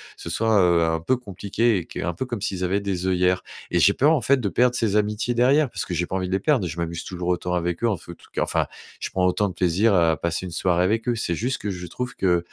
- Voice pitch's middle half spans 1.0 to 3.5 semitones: No, average, 4.5 semitones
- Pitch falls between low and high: No, very low, 95 Hz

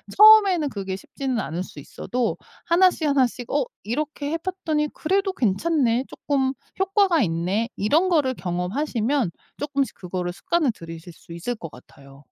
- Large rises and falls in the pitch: Yes, wide, 8.9 semitones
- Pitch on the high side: Yes, very high, 260 Hz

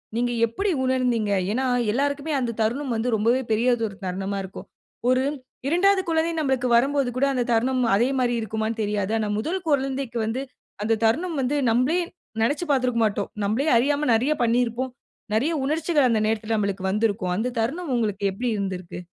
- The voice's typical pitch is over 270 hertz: No, high, 240 Hz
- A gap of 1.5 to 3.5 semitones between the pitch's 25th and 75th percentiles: No, average, 4.1 semitones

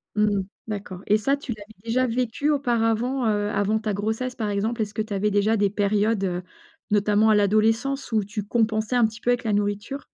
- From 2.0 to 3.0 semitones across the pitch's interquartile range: Yes, narrow, 2.4 semitones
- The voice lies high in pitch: Yes, high, 215 Hz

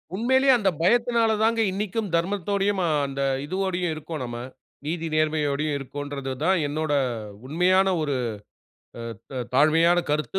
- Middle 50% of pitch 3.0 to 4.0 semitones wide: No, average, 5.0 semitones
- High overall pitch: No, medium, 170 Hz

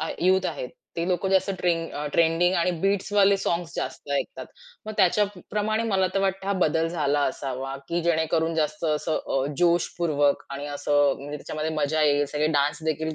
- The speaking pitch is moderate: Yes, medium, 165 Hz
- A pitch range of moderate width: Yes, average, 3.8 semitones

